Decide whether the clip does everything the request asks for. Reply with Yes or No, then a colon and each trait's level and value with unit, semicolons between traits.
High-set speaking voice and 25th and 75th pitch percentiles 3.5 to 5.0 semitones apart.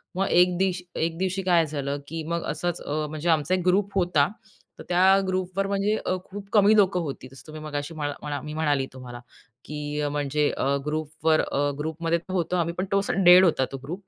No: medium, 165 Hz; average, 3.9 semitones